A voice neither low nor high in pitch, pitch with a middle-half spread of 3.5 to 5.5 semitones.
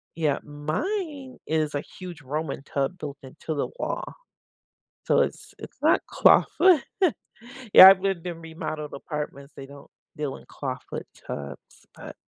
Yes: medium, 155 Hz; average, 4.4 semitones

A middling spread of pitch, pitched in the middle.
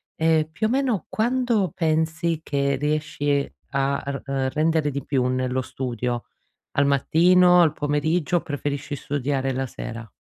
Yes: average, 3.2 semitones; medium, 145 Hz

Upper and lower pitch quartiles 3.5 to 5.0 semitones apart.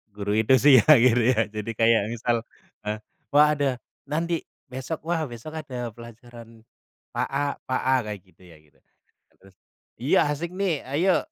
Yes: average, 4.6 semitones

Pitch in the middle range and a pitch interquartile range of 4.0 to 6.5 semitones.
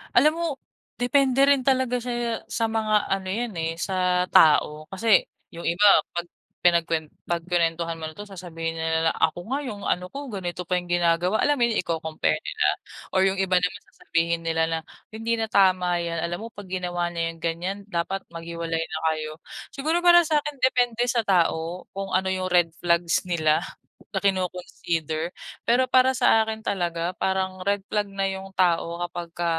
Yes: medium, 180 Hz; average, 4.5 semitones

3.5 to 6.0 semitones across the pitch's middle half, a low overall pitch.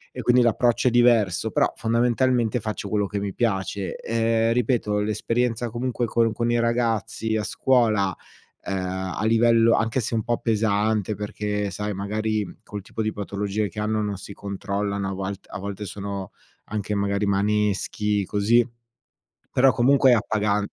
No: narrow, 2.4 semitones; low, 105 Hz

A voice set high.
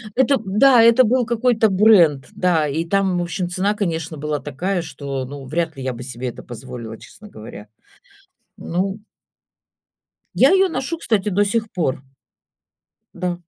No: medium, 180 Hz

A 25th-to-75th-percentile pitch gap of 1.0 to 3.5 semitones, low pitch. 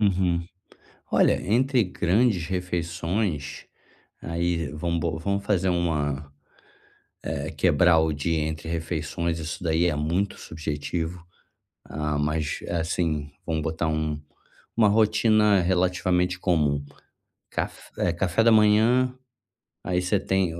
Yes: average, 3.1 semitones; very low, 85 Hz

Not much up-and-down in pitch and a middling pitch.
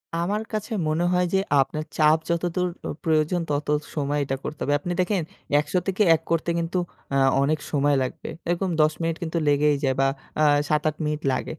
No: average, 3.1 semitones; medium, 155 Hz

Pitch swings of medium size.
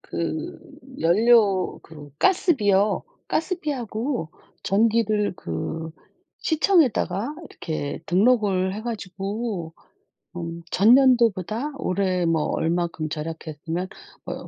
No: wide, 5.8 semitones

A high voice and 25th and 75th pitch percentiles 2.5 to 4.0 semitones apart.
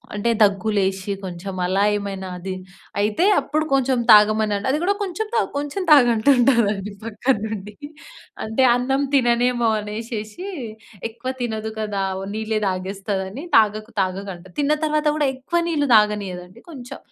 No: high, 220 Hz; average, 4.7 semitones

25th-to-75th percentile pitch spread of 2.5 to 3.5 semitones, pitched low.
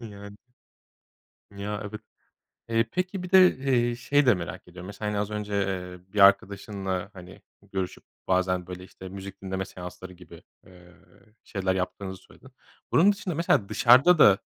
No: average, 4.0 semitones; low, 100 Hz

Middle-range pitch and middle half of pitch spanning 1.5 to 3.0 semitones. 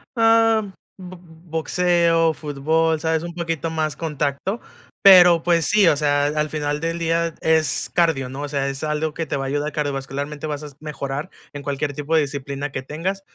Yes: medium, 155 Hz; average, 2.7 semitones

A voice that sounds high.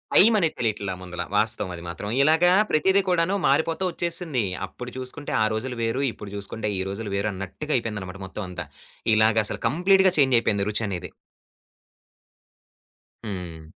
No: low, 110 Hz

